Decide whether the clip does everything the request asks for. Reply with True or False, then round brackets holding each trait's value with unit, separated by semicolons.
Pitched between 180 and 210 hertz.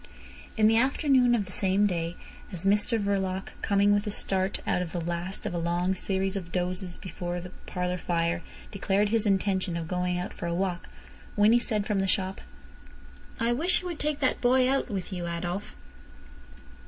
True (190 Hz)